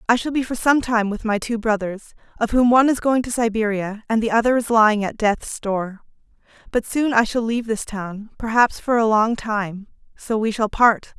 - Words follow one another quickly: Yes, fast, 220 wpm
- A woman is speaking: Yes, female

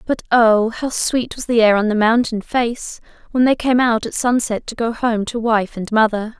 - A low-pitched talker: No, high, 230 Hz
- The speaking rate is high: Yes, fast, 225 wpm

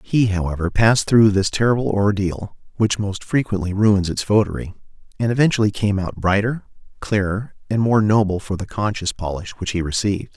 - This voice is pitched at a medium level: No, low, 100 Hz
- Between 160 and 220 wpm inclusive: Yes, average, 170 wpm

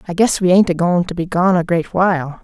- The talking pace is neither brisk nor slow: No, fast, 295 wpm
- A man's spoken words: No, female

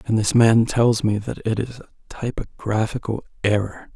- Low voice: Yes, low, 110 Hz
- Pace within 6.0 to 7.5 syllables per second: No, 4.7 syllables/s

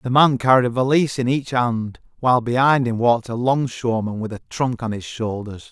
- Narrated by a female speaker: No, male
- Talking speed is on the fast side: Yes, fast, 210 wpm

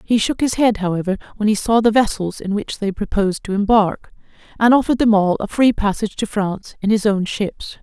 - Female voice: Yes, female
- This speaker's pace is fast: Yes, fast, 220 wpm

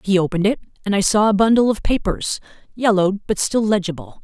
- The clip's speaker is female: Yes, female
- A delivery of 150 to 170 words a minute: No, average, 200 wpm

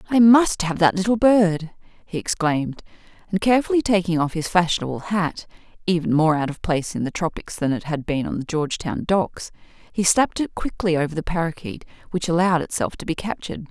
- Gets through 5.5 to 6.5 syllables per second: Yes, 5.8 syllables/s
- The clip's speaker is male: No, female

